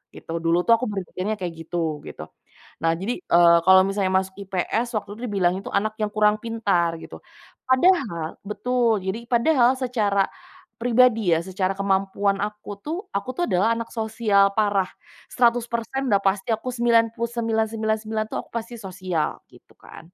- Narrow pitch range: No, average, 3.5 semitones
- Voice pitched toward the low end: No, high, 210 Hz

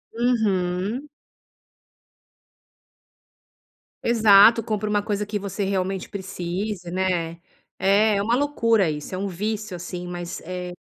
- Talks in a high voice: Yes, high, 200 Hz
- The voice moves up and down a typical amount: Yes, average, 3.1 semitones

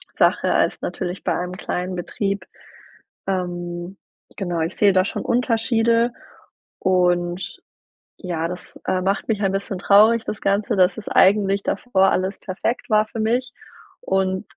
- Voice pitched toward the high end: Yes, high, 195 Hz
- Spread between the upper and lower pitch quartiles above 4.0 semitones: No, average, 2.9 semitones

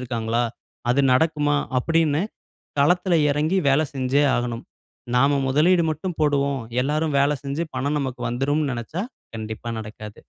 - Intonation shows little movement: No, average, 3.5 semitones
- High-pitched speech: No, medium, 140 Hz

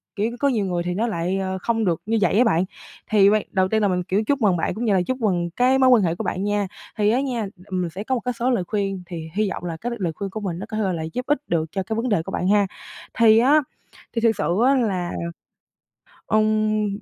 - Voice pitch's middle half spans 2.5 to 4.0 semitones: Yes, average, 3.7 semitones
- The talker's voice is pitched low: No, high, 205 Hz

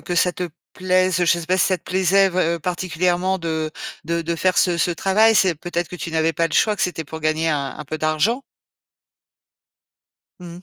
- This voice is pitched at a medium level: Yes, medium, 175 Hz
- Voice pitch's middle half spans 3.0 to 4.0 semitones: No, narrow, 2.4 semitones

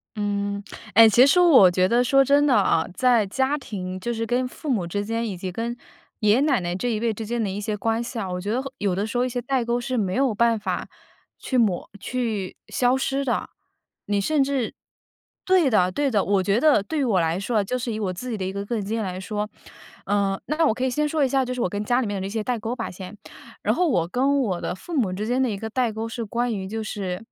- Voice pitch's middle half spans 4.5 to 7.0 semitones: No, average, 4.1 semitones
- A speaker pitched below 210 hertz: No, high, 225 Hz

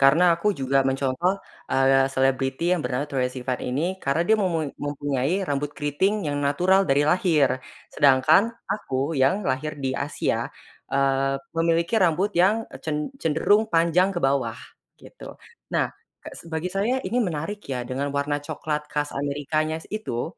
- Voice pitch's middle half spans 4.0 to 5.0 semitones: Yes, average, 4.4 semitones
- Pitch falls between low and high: Yes, medium, 145 Hz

